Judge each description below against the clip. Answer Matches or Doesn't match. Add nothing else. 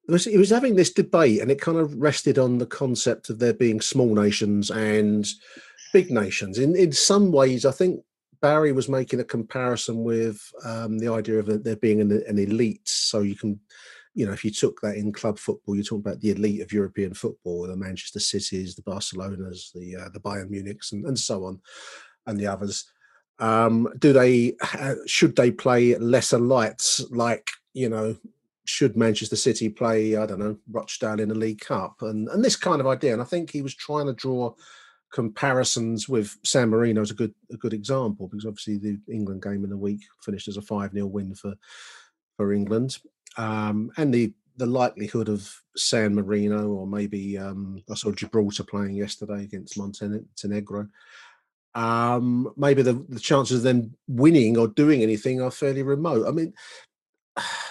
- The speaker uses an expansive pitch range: Doesn't match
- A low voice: Matches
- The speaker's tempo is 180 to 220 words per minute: Matches